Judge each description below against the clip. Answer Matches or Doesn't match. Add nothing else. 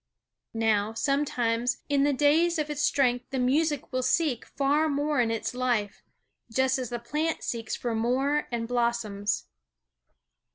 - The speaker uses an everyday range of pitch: Matches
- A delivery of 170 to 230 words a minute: Doesn't match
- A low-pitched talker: Doesn't match